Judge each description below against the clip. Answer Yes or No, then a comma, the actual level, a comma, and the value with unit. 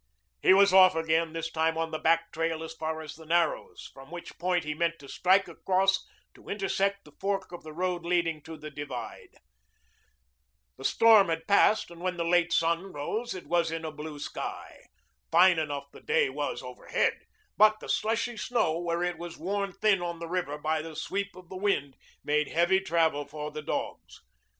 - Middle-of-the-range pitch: Yes, medium, 170 Hz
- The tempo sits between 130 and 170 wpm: No, average, 195 wpm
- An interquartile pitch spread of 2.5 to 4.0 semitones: Yes, average, 3.2 semitones